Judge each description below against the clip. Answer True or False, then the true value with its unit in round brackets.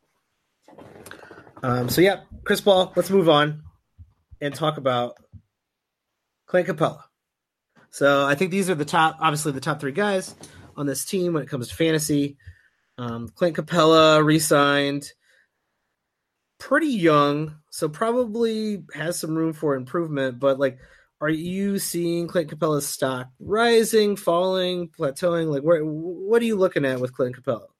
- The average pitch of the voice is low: False (160 Hz)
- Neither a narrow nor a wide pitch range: True (4.4 semitones)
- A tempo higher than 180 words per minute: False (145 wpm)